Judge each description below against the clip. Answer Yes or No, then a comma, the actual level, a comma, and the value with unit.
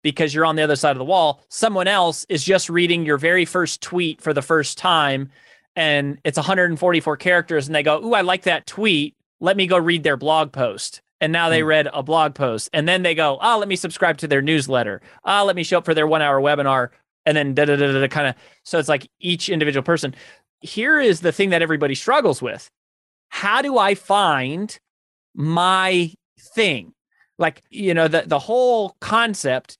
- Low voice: No, medium, 160 Hz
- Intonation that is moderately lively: Yes, average, 3.8 semitones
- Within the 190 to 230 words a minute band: Yes, average, 200 wpm